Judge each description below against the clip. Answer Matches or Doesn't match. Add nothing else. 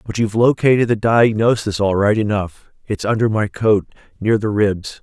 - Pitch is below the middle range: Matches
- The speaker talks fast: Doesn't match